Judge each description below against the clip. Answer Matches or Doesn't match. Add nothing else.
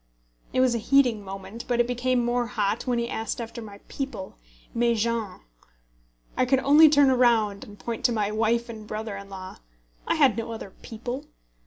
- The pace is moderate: Matches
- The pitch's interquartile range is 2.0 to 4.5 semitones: Matches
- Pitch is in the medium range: Doesn't match